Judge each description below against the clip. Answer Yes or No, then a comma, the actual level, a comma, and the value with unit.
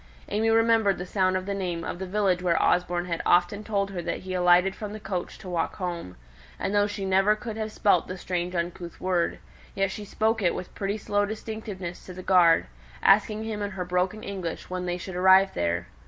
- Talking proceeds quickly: Yes, fast, 215 wpm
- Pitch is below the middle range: No, high, 190 Hz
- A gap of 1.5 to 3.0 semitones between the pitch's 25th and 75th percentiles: Yes, narrow, 2.5 semitones